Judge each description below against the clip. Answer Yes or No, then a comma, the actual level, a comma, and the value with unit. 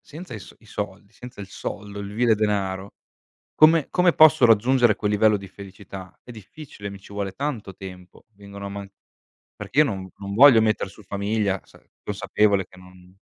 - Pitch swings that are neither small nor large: Yes, average, 3.1 semitones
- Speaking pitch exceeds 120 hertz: No, low, 100 Hz